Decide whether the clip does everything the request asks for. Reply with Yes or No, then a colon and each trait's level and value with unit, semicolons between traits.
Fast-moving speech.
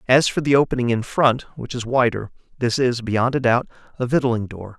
Yes: fast, 215 wpm